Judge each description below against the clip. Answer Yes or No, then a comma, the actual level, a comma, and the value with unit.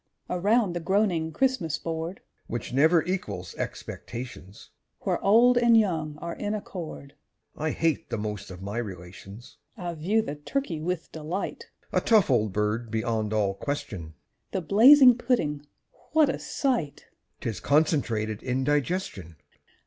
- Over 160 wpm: No, average, 140 wpm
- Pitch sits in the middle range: Yes, medium, 155 Hz